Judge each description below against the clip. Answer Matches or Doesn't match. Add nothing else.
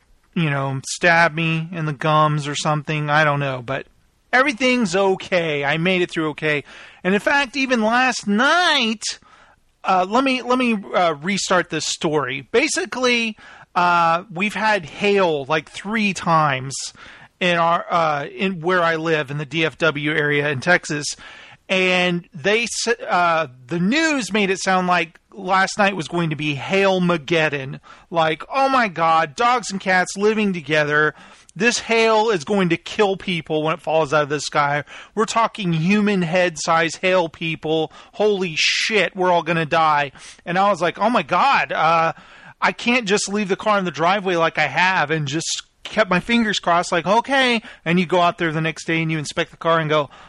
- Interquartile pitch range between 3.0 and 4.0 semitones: Doesn't match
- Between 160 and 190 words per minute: Matches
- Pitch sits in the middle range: Matches